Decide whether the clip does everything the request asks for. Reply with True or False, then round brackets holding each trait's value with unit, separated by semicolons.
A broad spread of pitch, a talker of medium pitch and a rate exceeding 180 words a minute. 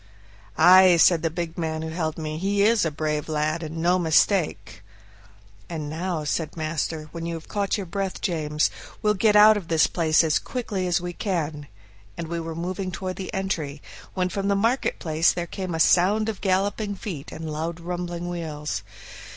False (3.2 semitones; 170 Hz; 190 wpm)